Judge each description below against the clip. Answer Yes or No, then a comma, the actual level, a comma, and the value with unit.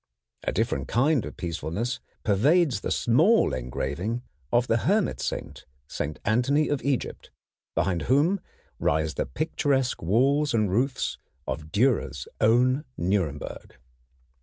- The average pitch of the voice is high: No, low, 120 Hz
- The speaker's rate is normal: No, slow, 115 wpm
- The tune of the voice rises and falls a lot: Yes, wide, 8.5 semitones